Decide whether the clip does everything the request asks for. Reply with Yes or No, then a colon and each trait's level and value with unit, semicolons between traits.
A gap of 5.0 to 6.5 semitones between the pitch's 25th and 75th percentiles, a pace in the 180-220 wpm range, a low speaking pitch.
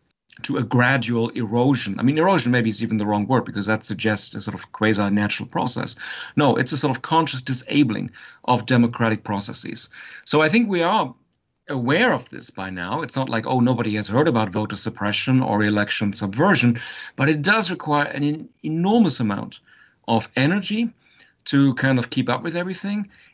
Yes: wide, 5.5 semitones; average, 185 wpm; low, 125 Hz